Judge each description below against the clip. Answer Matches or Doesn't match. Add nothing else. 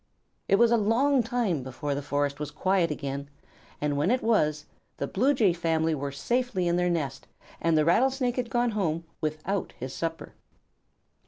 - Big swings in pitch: Matches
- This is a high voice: Doesn't match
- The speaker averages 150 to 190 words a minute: Matches